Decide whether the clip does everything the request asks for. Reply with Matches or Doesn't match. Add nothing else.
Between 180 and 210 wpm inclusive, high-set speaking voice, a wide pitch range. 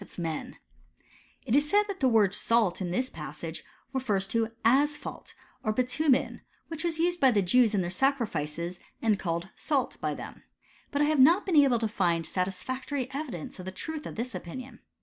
Matches